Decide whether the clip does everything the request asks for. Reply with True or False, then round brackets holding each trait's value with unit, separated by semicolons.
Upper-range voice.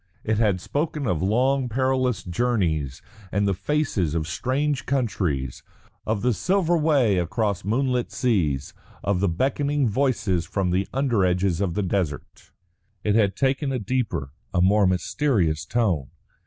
False (105 Hz)